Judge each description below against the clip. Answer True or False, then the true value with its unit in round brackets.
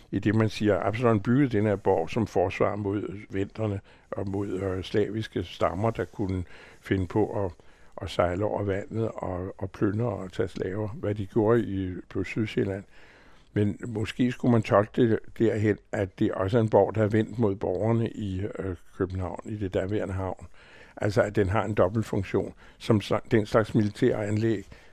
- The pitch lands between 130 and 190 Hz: False (105 Hz)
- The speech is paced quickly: False (185 wpm)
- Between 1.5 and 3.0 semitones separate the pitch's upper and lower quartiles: True (2.4 semitones)